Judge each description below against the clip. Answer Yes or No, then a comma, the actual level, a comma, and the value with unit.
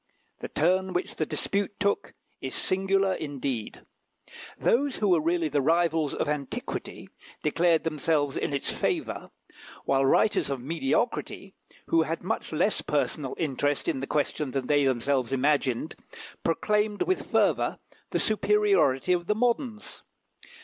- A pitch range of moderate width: No, wide, 5.9 semitones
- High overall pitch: No, medium, 160 Hz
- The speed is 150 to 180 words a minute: No, slow, 135 wpm